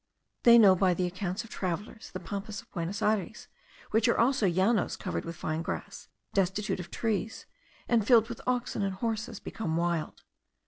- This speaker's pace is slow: No, average, 175 wpm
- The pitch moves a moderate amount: Yes, average, 3.7 semitones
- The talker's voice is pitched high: Yes, high, 200 Hz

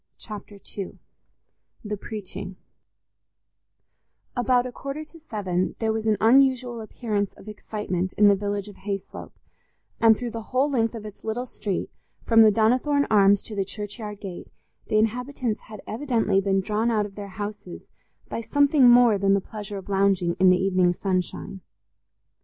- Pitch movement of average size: Yes, average, 3.0 semitones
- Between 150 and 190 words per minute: Yes, average, 160 wpm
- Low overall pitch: No, high, 210 Hz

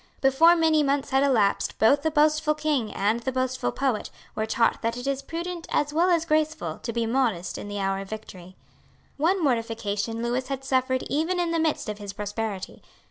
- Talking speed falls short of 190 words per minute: No, average, 195 wpm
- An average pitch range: No, wide, 5.8 semitones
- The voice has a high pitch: Yes, very high, 260 Hz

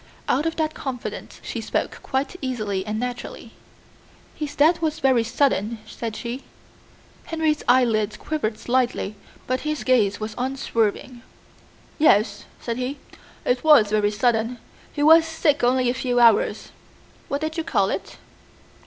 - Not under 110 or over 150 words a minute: Yes, average, 145 wpm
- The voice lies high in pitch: Yes, very high, 250 Hz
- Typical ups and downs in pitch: Yes, average, 4.6 semitones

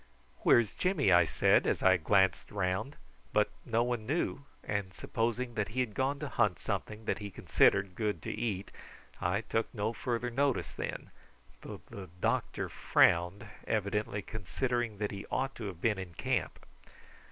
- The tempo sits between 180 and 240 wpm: No, average, 165 wpm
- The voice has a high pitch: No, low, 105 Hz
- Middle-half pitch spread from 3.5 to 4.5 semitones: Yes, average, 3.8 semitones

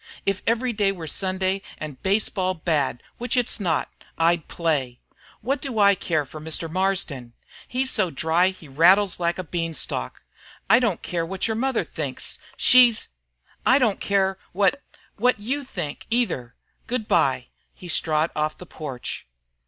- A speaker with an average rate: Yes, average, 155 wpm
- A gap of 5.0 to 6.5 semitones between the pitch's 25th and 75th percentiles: Yes, average, 5.3 semitones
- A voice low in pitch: No, medium, 185 Hz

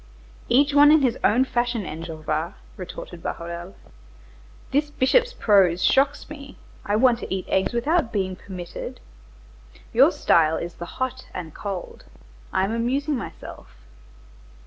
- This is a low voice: No, high, 225 Hz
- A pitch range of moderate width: No, wide, 7.1 semitones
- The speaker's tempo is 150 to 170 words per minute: No, slow, 135 wpm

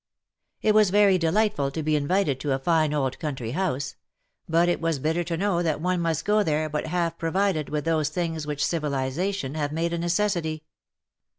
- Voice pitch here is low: No, medium, 165 Hz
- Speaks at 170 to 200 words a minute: Yes, average, 190 wpm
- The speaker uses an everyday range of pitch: Yes, average, 3.1 semitones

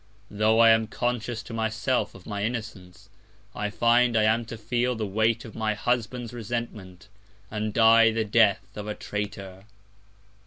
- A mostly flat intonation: Yes, narrow, 1.9 semitones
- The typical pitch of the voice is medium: No, low, 110 Hz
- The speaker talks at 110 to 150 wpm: No, average, 160 wpm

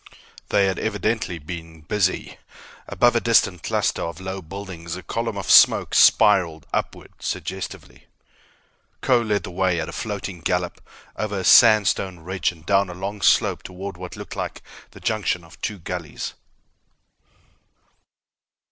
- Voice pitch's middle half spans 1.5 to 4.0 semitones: Yes, average, 3.0 semitones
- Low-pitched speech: Yes, very low, 95 Hz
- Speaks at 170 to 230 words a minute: No, average, 145 wpm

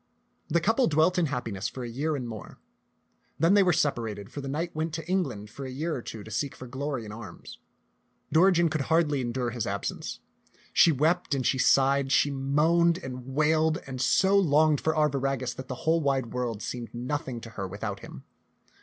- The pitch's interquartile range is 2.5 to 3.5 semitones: No, average, 4.7 semitones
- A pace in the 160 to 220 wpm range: Yes, fast, 205 wpm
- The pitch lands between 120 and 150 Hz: Yes, medium, 140 Hz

